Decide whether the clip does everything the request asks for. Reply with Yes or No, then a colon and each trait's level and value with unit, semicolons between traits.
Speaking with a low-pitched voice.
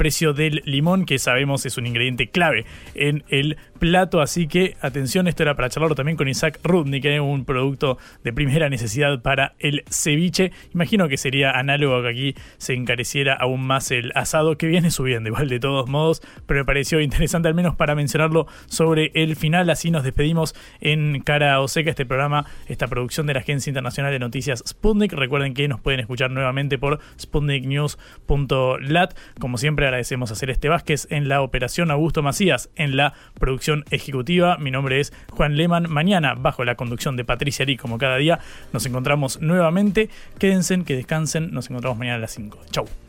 No: medium, 145 Hz